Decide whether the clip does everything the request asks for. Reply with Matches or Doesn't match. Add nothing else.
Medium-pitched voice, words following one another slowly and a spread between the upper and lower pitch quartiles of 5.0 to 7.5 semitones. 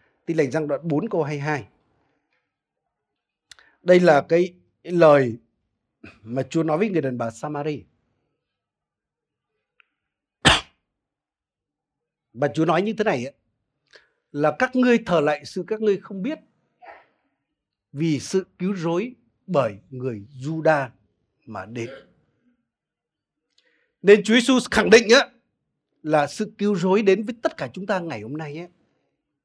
Matches